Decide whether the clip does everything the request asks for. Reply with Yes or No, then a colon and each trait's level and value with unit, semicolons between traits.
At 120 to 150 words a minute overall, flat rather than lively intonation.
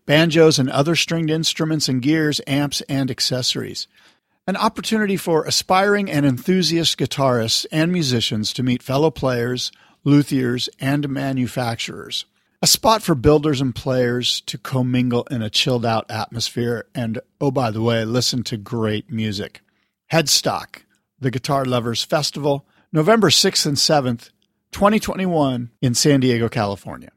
No: slow, 135 wpm; average, 4.6 semitones